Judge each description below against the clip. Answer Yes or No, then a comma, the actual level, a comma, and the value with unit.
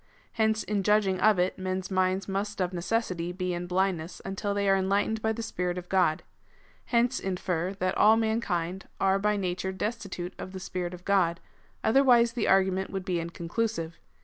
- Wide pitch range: No, average, 2.7 semitones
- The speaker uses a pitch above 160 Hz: Yes, high, 190 Hz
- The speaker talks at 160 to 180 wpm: Yes, average, 175 wpm